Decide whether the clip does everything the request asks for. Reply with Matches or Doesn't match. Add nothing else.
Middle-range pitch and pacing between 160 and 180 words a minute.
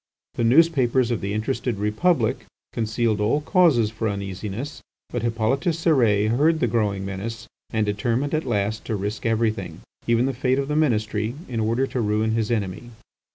Doesn't match